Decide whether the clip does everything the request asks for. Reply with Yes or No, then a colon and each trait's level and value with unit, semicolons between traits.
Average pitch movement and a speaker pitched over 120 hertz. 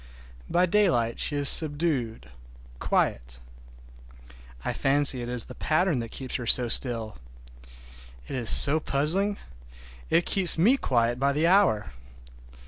No: wide, 6.1 semitones; medium, 140 Hz